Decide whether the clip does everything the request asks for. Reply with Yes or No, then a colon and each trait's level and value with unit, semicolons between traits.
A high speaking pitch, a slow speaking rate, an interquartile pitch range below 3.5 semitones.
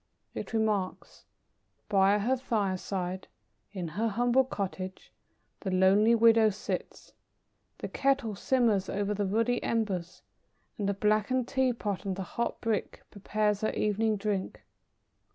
Yes: high, 210 Hz; slow, 130 wpm; average, 2.9 semitones